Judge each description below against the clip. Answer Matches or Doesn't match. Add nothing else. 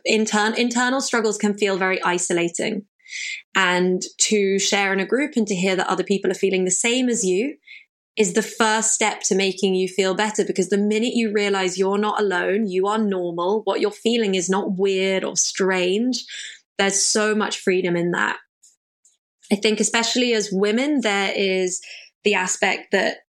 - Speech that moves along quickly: Doesn't match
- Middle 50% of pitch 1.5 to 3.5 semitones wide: Matches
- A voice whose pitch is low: Doesn't match